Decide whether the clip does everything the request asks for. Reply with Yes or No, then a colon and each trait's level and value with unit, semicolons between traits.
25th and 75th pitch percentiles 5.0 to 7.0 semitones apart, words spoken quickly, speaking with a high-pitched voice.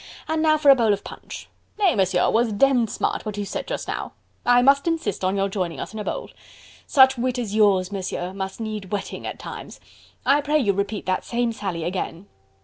Yes: wide, 5.4 semitones; fast, 215 wpm; high, 215 Hz